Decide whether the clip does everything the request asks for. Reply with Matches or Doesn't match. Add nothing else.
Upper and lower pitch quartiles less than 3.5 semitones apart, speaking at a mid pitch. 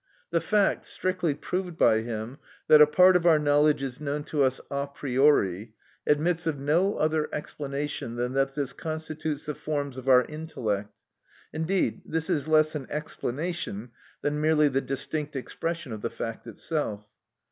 Matches